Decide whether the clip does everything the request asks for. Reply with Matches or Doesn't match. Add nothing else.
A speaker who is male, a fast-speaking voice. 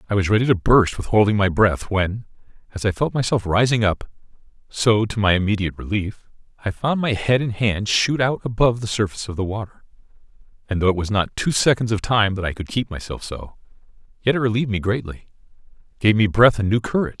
Matches